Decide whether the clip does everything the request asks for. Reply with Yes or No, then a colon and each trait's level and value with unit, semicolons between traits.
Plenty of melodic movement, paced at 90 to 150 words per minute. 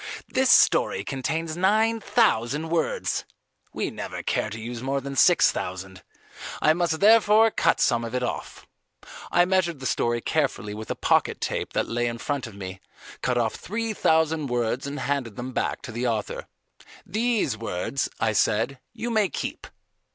No: wide, 7.1 semitones; average, 170 wpm